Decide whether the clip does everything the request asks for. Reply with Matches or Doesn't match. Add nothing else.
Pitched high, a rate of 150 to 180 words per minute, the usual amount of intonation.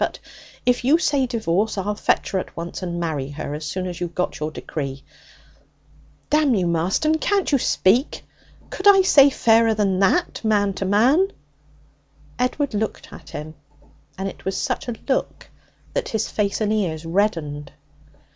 Doesn't match